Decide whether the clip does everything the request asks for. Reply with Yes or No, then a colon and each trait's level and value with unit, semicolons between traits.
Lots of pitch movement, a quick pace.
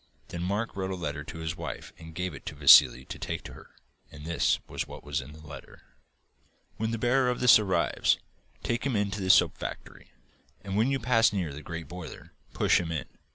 Yes: wide, 5.8 semitones; fast, 215 wpm